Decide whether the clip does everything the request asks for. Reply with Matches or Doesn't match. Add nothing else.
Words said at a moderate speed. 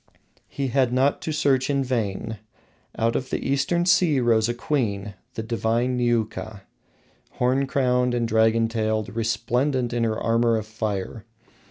Matches